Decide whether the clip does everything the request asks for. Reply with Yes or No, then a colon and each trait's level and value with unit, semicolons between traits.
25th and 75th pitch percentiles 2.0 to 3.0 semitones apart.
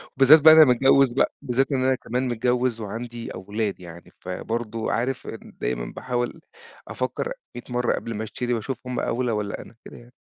Yes: average, 2.7 semitones